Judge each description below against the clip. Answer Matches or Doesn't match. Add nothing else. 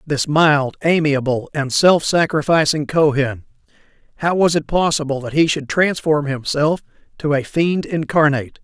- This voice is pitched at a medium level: Matches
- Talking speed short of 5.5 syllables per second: Matches